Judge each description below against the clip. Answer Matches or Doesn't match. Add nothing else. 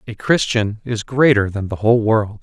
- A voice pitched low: Matches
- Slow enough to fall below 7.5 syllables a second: Matches